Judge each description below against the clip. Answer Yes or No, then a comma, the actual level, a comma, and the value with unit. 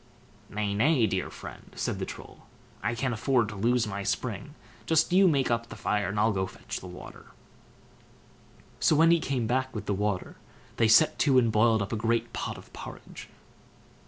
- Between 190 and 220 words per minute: Yes, average, 195 wpm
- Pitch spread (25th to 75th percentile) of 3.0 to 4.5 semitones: Yes, average, 3.9 semitones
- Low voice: Yes, low, 115 Hz